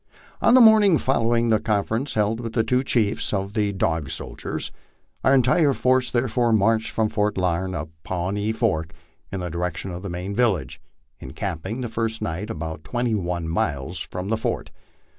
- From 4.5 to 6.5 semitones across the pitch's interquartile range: Yes, average, 5.1 semitones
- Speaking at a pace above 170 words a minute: Yes, average, 180 wpm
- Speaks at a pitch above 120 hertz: No, low, 105 Hz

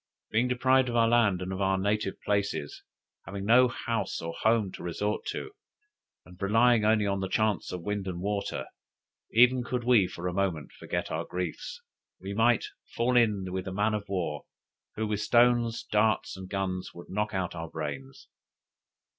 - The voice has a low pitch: Yes, low, 105 Hz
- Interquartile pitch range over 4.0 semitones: No, average, 3.7 semitones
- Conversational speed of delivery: Yes, average, 180 wpm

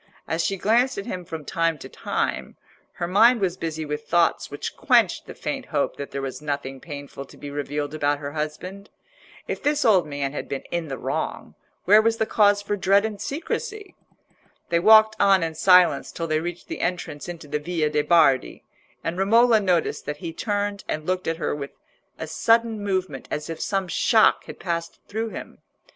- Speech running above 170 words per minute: Yes, average, 195 wpm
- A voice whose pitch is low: No, medium, 175 Hz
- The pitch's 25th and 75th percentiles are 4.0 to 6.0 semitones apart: Yes, average, 5.1 semitones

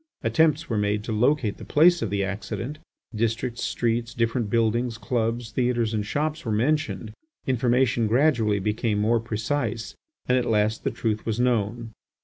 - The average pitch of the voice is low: Yes, low, 115 Hz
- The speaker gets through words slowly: No, average, 155 wpm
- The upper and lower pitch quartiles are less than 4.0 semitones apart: Yes, narrow, 2.6 semitones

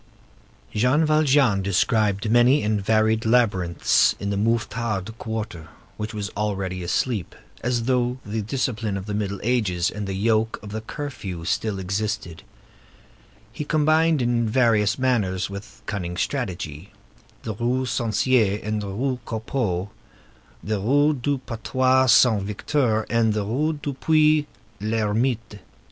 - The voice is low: Yes, low, 110 Hz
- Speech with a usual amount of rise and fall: Yes, average, 3.8 semitones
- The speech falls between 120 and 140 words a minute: Yes, slow, 135 wpm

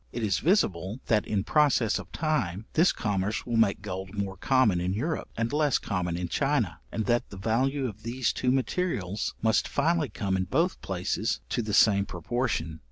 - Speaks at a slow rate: No, average, 185 wpm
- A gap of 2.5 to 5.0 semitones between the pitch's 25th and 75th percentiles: No, wide, 5.4 semitones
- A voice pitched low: Yes, low, 110 Hz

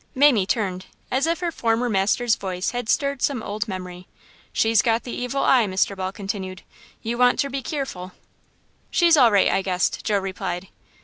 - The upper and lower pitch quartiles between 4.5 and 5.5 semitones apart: Yes, average, 4.8 semitones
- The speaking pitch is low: No, high, 220 Hz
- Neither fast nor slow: Yes, average, 175 wpm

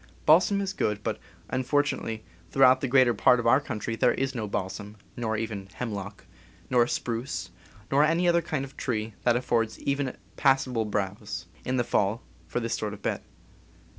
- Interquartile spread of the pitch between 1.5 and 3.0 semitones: No, average, 3.7 semitones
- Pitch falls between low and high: No, low, 120 Hz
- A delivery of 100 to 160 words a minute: No, average, 170 wpm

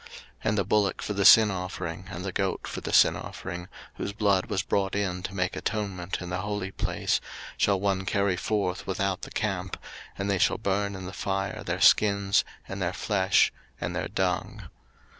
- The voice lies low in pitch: Yes, very low, 95 Hz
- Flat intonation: Yes, narrow, 1.4 semitones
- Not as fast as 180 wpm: No, average, 195 wpm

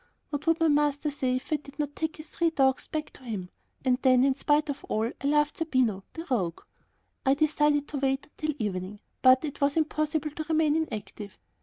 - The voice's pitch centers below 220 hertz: No, very high, 290 Hz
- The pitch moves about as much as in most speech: Yes, average, 3.0 semitones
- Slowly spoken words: No, fast, 205 wpm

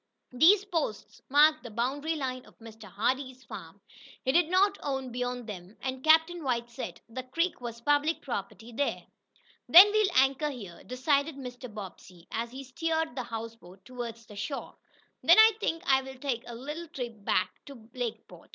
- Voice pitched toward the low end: No, very high, 260 Hz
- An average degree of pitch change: Yes, average, 4.6 semitones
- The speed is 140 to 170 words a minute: Yes, average, 165 wpm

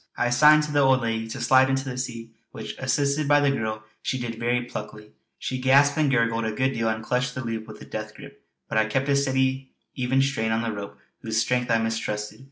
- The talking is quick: Yes, fast, 235 wpm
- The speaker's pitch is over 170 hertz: No, low, 125 Hz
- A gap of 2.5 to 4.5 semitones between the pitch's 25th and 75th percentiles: Yes, average, 3.0 semitones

